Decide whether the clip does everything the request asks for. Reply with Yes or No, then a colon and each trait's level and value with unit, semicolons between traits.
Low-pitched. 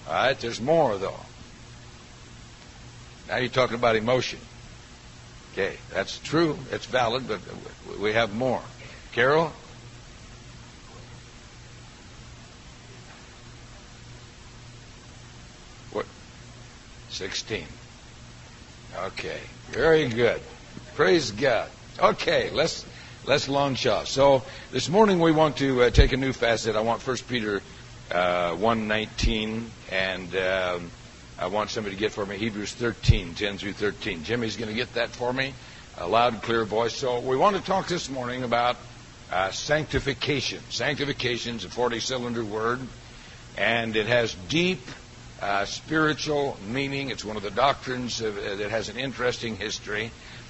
Yes: low, 120 Hz